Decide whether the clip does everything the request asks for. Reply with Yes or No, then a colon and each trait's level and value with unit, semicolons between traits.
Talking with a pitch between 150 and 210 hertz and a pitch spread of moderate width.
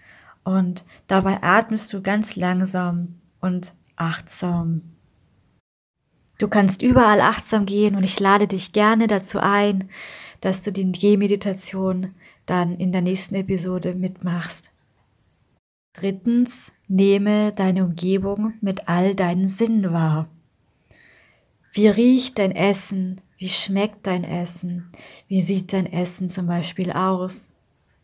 No: high, 190 Hz; narrow, 2.1 semitones